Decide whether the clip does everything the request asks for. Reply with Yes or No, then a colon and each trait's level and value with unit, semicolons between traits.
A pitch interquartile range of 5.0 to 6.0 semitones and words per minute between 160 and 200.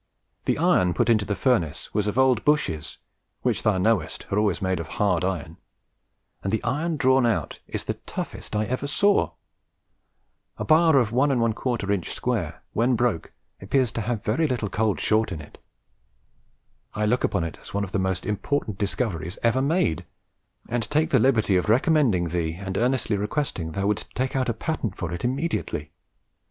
Yes: wide, 5.4 semitones; average, 175 wpm